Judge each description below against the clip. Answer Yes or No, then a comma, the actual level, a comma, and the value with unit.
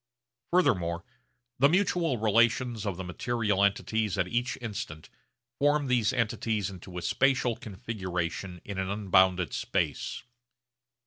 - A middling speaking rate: No, slow, 120 wpm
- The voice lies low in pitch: Yes, low, 105 Hz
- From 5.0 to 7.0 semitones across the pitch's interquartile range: No, average, 4.6 semitones